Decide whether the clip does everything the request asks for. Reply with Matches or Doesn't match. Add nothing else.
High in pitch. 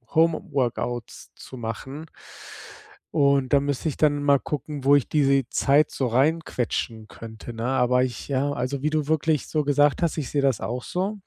Doesn't match